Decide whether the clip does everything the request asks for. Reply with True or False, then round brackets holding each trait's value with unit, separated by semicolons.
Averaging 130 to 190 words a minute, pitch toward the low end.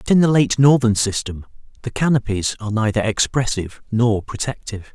True (160 wpm; 115 Hz)